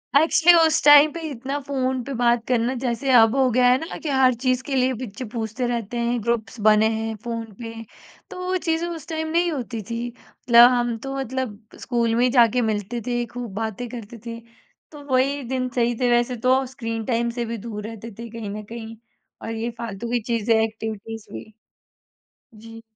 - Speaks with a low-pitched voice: No, high, 240 Hz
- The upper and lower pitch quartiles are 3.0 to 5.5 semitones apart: No, narrow, 2.5 semitones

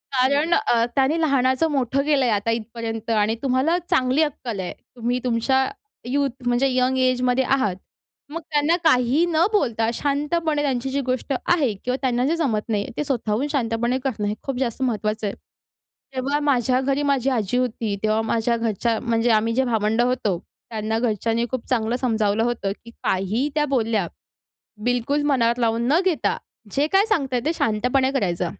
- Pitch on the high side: Yes, very high, 250 Hz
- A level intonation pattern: No, average, 3.4 semitones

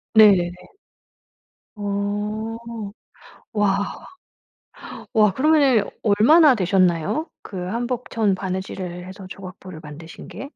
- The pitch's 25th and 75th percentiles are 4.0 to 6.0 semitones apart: No, average, 3.3 semitones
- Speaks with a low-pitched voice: No, high, 200 Hz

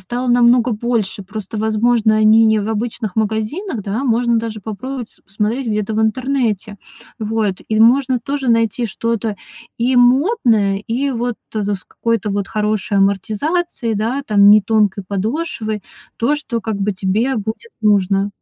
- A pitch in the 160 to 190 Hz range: No, high, 220 Hz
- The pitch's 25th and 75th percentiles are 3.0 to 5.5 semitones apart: No, narrow, 2.6 semitones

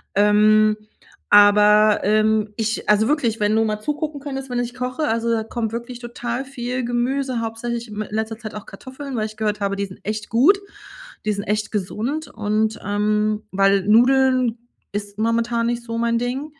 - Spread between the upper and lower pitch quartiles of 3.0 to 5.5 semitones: No, narrow, 2.5 semitones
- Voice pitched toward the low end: No, high, 225 Hz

